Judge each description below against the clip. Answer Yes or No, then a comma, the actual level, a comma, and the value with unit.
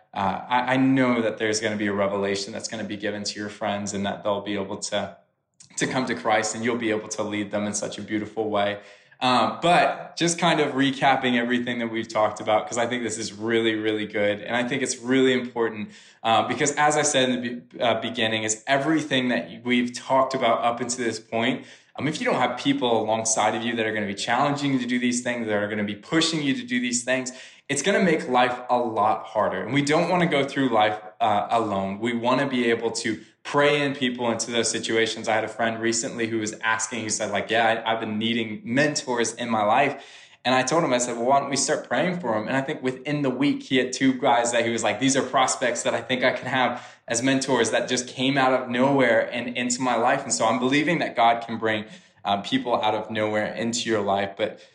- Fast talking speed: Yes, fast, 250 wpm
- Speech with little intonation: No, average, 3.3 semitones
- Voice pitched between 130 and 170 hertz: No, low, 120 Hz